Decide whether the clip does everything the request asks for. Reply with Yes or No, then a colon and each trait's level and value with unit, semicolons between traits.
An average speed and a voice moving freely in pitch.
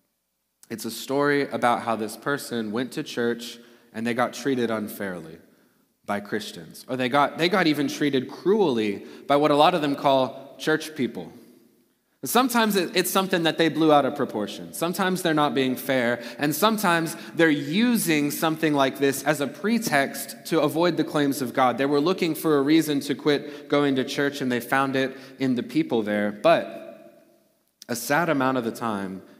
No: average, 185 wpm; average, 4.8 semitones